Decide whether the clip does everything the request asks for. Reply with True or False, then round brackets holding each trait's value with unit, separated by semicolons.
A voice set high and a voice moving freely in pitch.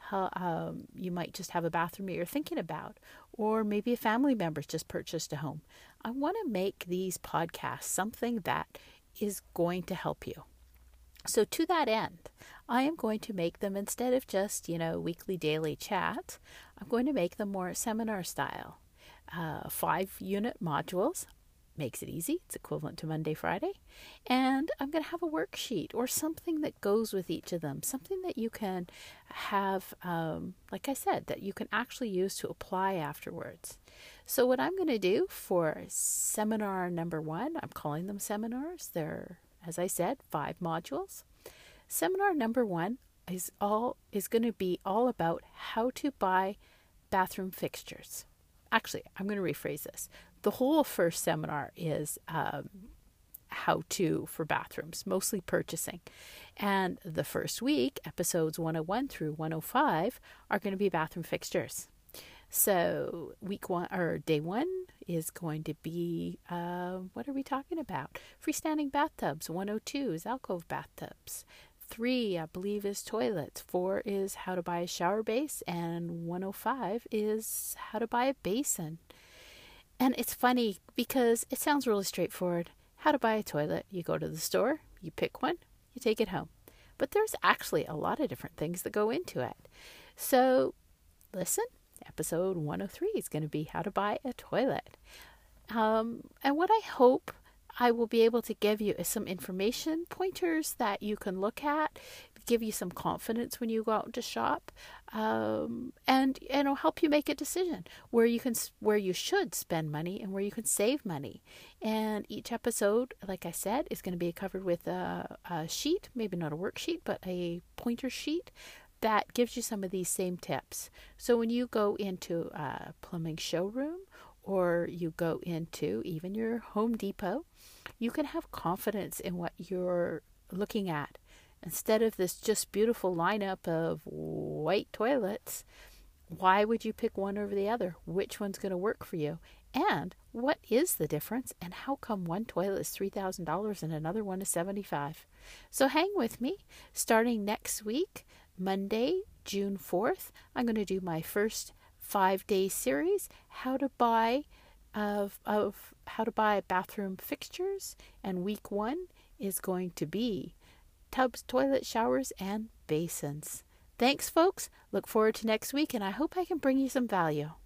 True (210 Hz; 5.9 semitones)